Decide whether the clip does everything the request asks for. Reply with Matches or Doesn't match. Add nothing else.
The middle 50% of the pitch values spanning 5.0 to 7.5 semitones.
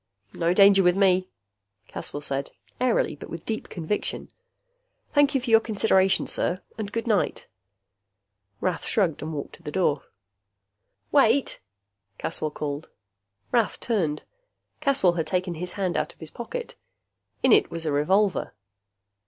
Matches